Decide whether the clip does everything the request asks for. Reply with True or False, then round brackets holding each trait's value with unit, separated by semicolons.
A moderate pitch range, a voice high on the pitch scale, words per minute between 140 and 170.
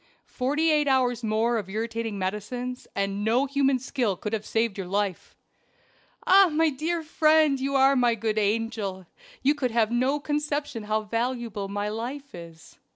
True (4.8 semitones; 235 Hz; 160 wpm)